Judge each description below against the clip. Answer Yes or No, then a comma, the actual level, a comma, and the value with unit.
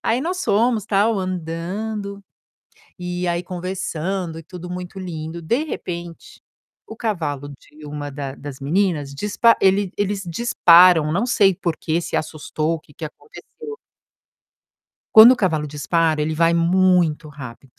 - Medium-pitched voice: Yes, medium, 175 Hz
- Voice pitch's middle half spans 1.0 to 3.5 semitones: No, average, 4.1 semitones